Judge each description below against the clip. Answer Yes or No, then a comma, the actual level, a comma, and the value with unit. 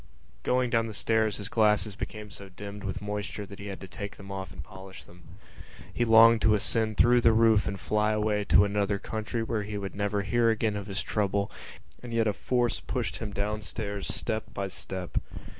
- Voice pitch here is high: No, low, 105 Hz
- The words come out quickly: Yes, fast, 210 wpm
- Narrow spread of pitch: Yes, narrow, 1.9 semitones